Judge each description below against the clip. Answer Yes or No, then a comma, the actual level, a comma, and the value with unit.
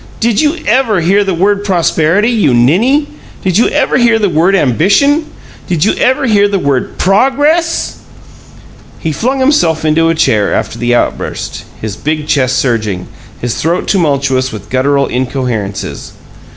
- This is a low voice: No, medium, 170 Hz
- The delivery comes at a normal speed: Yes, average, 150 wpm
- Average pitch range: No, wide, 9.0 semitones